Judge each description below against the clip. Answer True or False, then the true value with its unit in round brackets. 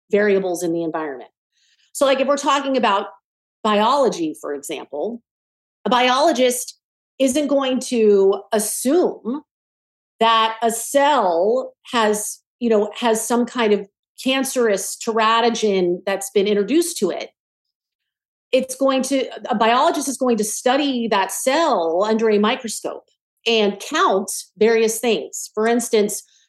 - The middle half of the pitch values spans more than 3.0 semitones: True (3.9 semitones)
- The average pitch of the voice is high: True (230 Hz)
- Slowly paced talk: True (125 wpm)